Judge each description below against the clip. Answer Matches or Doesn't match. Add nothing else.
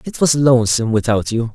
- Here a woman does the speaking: Doesn't match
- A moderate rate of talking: Matches